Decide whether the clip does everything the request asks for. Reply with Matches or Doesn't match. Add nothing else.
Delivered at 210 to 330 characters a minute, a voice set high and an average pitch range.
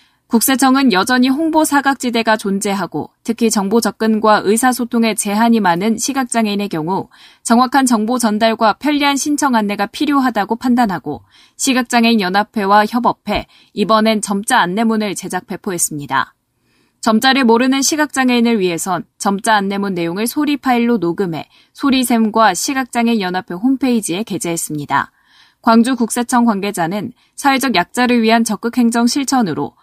Doesn't match